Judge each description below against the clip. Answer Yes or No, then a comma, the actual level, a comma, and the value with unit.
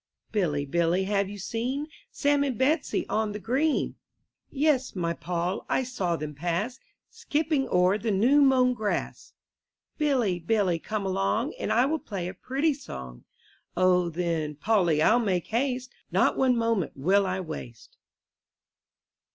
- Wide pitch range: Yes, wide, 6.7 semitones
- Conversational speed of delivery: Yes, average, 145 wpm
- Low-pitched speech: No, high, 210 Hz